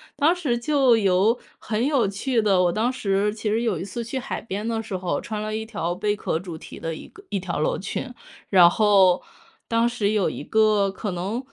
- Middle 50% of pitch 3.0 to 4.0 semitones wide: Yes, average, 3.4 semitones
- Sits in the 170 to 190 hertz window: No, high, 210 Hz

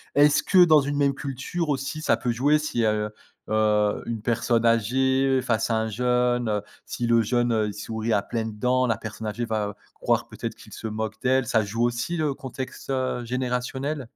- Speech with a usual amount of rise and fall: Yes, average, 3.1 semitones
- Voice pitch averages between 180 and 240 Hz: No, low, 120 Hz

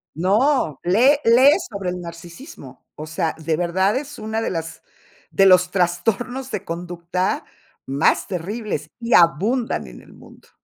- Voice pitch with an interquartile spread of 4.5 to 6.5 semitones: Yes, wide, 5.5 semitones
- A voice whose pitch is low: No, medium, 185 Hz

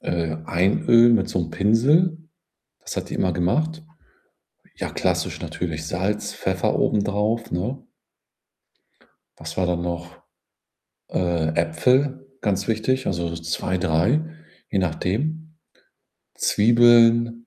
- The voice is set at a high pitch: No, low, 100 Hz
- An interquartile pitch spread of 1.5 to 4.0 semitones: No, wide, 5.4 semitones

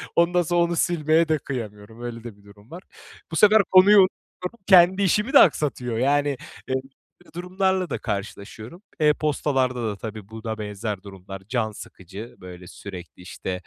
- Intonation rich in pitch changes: Yes, wide, 8.8 semitones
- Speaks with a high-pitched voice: No, low, 125 Hz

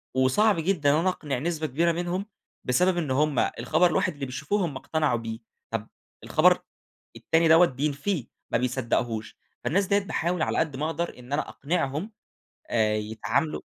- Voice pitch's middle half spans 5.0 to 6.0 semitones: Yes, average, 5.3 semitones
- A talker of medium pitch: Yes, medium, 150 Hz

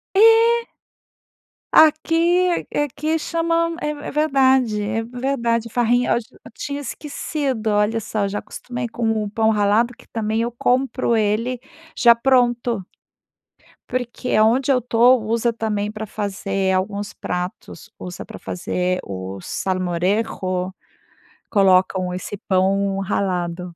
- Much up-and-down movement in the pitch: No, average, 4.4 semitones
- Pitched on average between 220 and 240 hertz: Yes, high, 225 Hz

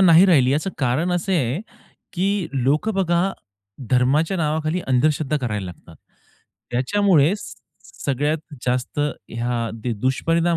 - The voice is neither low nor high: Yes, medium, 150 Hz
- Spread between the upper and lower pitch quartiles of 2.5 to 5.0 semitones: No, wide, 5.5 semitones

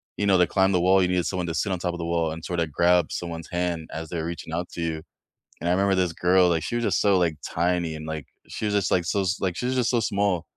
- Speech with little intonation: Yes, narrow, 2.3 semitones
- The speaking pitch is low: Yes, very low, 90 Hz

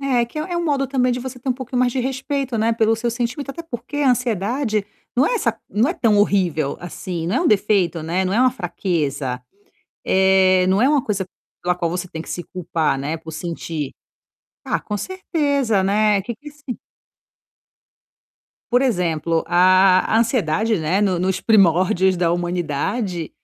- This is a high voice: Yes, high, 205 Hz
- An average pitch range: No, wide, 6.1 semitones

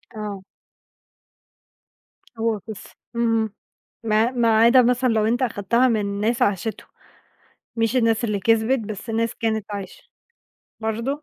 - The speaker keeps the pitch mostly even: Yes, narrow, 1.7 semitones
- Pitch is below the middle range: No, high, 225 Hz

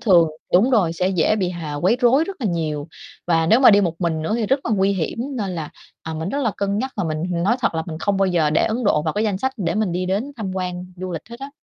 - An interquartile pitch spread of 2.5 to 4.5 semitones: No, average, 5.1 semitones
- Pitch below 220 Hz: Yes, high, 190 Hz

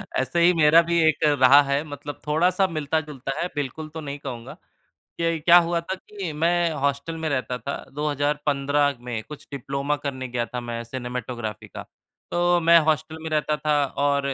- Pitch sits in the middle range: Yes, medium, 145 Hz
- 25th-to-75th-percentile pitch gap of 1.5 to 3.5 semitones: Yes, average, 2.8 semitones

